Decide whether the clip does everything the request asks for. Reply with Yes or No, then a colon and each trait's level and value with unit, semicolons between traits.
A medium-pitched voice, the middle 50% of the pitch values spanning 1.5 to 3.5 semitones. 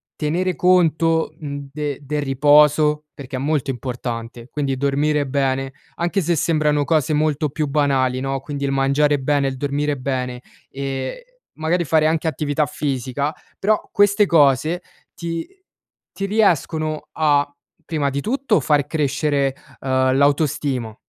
Yes: medium, 145 Hz; narrow, 2.5 semitones